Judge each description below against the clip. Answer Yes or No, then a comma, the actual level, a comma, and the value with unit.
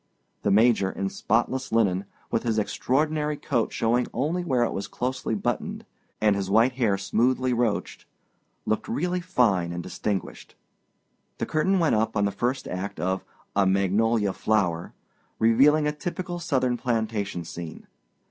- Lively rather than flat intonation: No, average, 4.8 semitones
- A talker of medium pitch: No, low, 115 Hz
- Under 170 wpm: Yes, average, 150 wpm